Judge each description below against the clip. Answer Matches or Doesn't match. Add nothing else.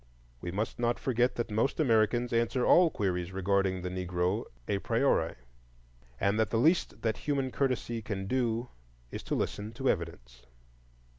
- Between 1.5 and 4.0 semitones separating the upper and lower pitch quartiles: Doesn't match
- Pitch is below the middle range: Matches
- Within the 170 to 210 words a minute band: Doesn't match